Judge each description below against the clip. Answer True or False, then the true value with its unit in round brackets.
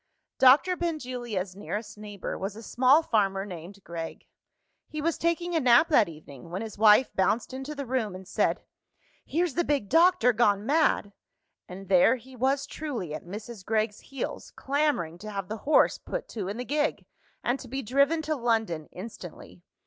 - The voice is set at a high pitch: True (230 Hz)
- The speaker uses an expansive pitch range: True (6.2 semitones)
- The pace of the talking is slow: False (175 wpm)